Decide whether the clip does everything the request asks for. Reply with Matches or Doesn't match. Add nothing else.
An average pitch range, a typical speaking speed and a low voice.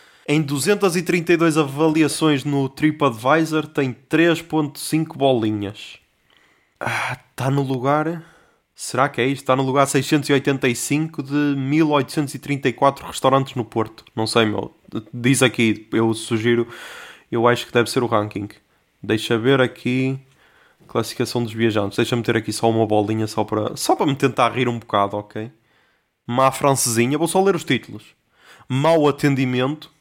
Matches